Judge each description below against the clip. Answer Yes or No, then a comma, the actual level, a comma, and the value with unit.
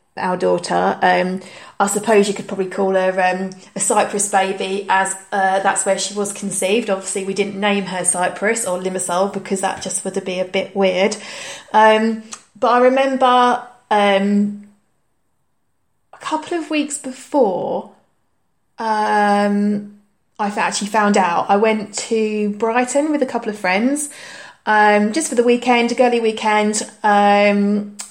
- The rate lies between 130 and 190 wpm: Yes, average, 155 wpm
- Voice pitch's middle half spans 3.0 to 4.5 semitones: No, narrow, 2.4 semitones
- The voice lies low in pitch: No, high, 205 Hz